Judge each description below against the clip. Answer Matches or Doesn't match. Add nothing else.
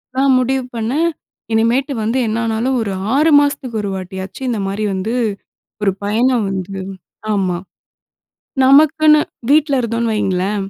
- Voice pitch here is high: Matches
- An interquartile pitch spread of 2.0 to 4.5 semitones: Doesn't match